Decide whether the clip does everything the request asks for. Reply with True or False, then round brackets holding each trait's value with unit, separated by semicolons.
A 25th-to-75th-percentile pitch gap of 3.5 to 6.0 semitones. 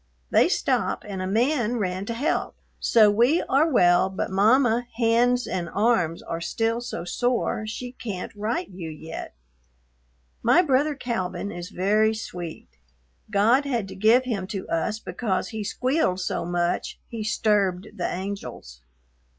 True (4.6 semitones)